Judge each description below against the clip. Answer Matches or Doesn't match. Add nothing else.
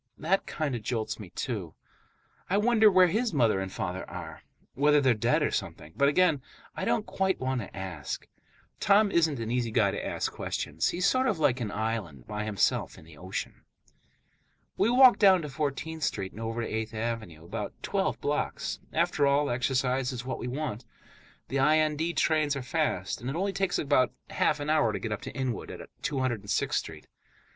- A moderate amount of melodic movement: Doesn't match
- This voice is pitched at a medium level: Doesn't match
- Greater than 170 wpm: Matches